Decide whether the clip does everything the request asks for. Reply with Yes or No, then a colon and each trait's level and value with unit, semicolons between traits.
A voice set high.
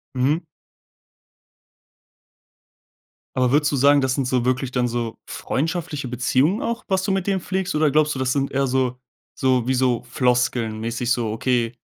No: low, 130 Hz